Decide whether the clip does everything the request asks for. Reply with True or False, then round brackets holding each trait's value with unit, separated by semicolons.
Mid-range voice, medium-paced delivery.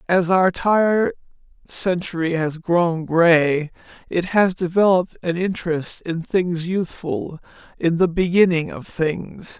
False (175 Hz; 120 wpm)